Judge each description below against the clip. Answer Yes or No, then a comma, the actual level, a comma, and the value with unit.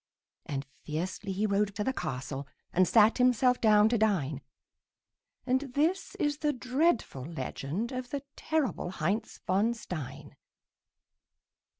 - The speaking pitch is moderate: No, high, 210 Hz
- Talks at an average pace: No, slow, 125 wpm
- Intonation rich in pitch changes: Yes, wide, 6.8 semitones